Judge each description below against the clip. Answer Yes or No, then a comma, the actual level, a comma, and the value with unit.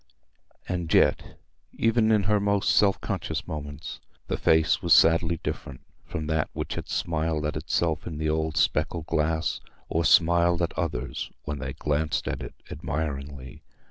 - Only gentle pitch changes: Yes, narrow, 2.1 semitones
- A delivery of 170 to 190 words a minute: No, average, 155 wpm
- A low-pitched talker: Yes, very low, 80 Hz